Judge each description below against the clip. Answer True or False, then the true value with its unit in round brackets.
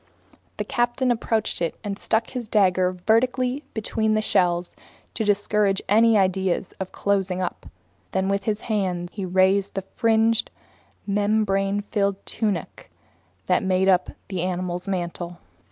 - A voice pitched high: True (200 Hz)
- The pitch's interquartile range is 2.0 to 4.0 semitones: True (2.8 semitones)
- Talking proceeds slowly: True (130 wpm)